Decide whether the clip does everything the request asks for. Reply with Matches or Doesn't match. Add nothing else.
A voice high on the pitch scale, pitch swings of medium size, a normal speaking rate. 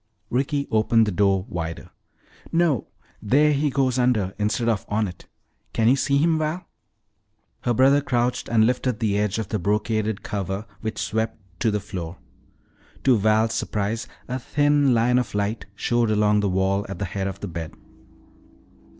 Doesn't match